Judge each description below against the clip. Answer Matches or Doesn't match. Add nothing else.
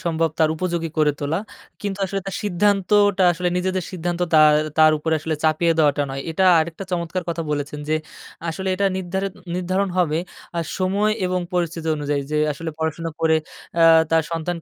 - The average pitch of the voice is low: Doesn't match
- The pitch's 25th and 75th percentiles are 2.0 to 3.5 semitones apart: Matches